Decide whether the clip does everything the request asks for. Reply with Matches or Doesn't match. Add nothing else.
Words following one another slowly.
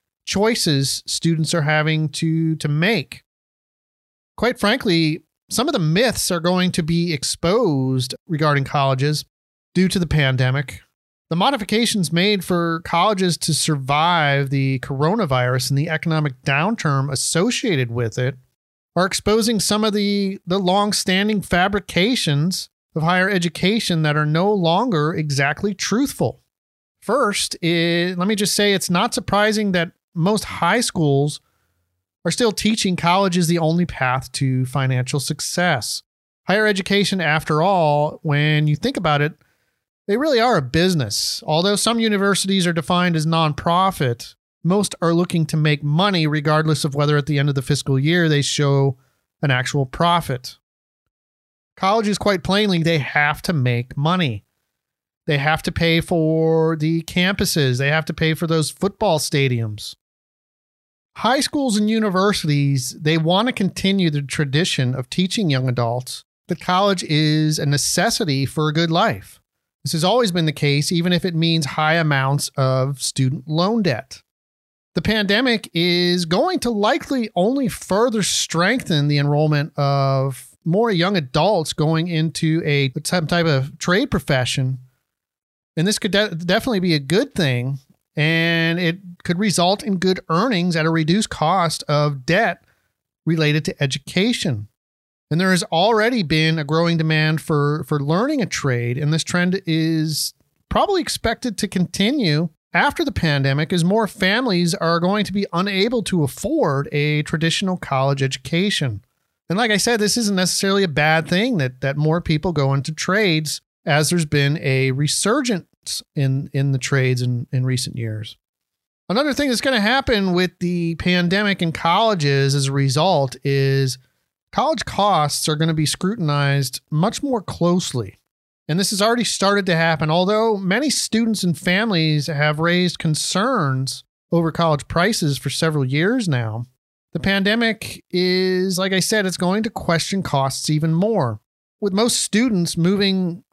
Doesn't match